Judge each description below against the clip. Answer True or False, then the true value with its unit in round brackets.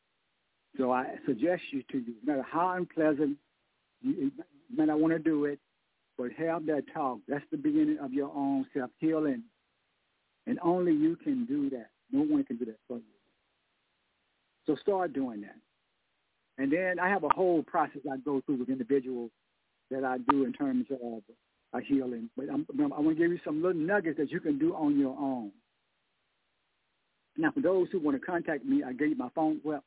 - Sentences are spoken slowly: False (195 wpm)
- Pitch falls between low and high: True (155 Hz)